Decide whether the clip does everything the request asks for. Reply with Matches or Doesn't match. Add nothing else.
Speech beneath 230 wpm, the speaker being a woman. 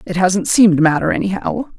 Matches